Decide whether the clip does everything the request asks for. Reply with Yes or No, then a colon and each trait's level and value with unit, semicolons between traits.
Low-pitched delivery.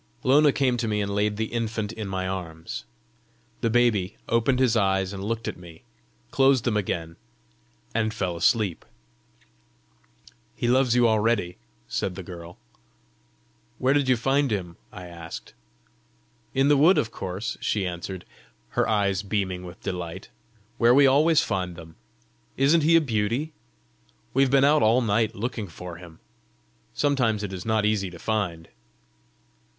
Yes: low, 110 Hz